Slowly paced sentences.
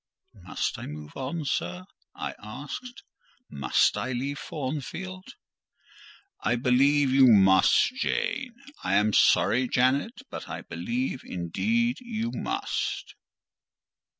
Yes: slow, 110 wpm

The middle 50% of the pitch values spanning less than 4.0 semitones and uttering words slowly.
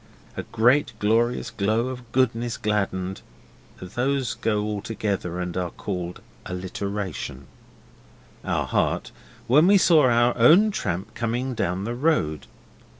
No: average, 4.6 semitones; slow, 125 wpm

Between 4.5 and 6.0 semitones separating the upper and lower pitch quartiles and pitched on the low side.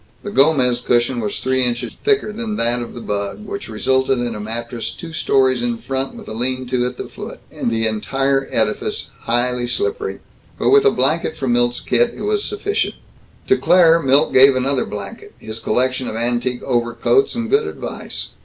Yes: average, 4.9 semitones; low, 130 Hz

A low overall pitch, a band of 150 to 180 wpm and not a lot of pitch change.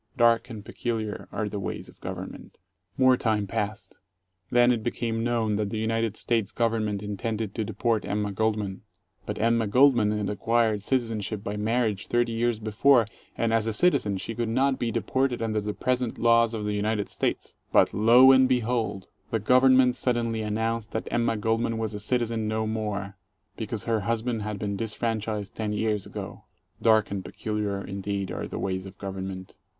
Yes: low, 110 Hz; average, 175 wpm; narrow, 2.1 semitones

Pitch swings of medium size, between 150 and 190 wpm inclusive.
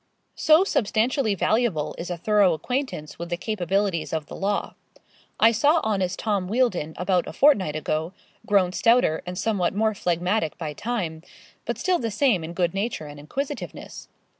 Yes: average, 4.9 semitones; average, 165 wpm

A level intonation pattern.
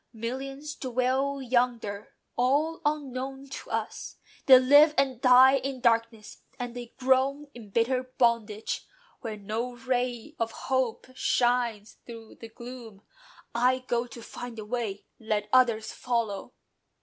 Yes: narrow, 2.3 semitones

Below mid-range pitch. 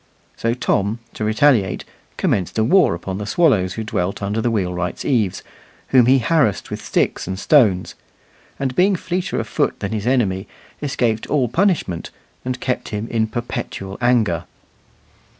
Yes: low, 110 Hz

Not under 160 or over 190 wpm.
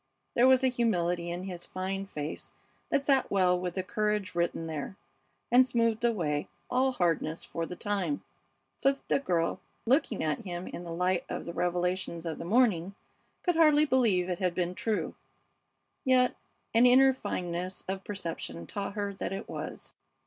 Yes: average, 170 wpm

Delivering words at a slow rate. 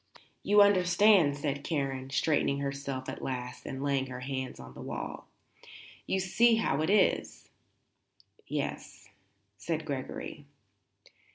Yes: slow, 120 wpm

